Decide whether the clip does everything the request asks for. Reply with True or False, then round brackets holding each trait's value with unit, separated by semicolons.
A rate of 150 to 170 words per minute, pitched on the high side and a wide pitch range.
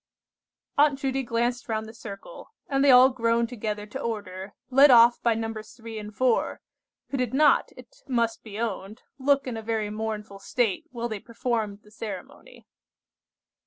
False (165 wpm; 230 Hz; 2.9 semitones)